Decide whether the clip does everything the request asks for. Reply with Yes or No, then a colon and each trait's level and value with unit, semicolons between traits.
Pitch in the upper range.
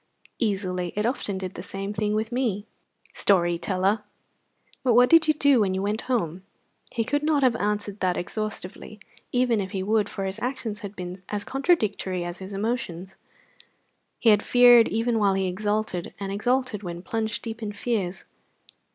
Yes: high, 210 Hz